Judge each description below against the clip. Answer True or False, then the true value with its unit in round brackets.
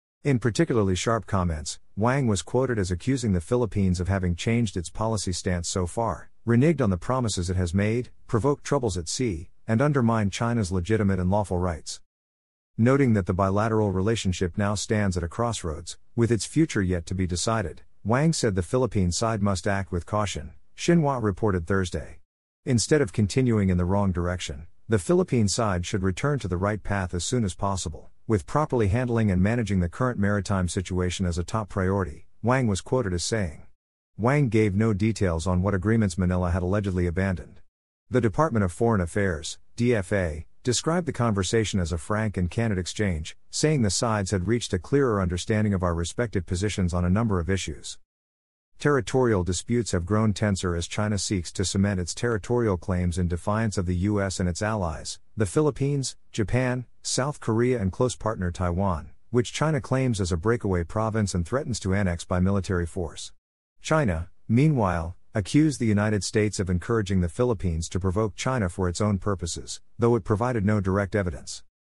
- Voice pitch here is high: False (100 Hz)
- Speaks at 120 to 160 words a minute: False (180 wpm)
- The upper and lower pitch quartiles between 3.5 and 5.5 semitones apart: True (4.2 semitones)